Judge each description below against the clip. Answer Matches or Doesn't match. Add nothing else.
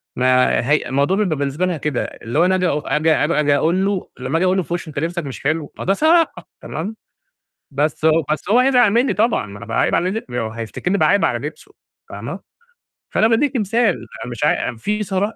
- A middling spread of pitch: Doesn't match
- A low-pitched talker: Doesn't match